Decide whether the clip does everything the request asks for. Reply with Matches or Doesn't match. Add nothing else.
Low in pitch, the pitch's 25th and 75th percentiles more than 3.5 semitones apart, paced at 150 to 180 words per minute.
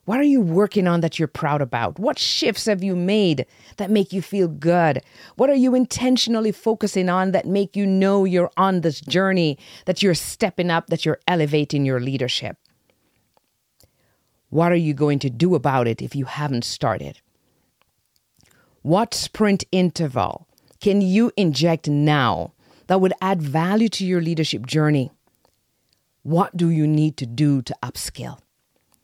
Doesn't match